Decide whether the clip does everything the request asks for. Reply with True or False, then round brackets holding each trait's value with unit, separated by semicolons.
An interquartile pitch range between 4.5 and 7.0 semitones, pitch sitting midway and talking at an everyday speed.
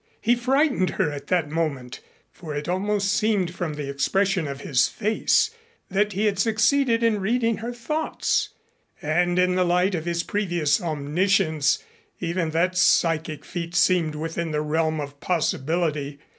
True (4.8 semitones; 175 Hz; 155 wpm)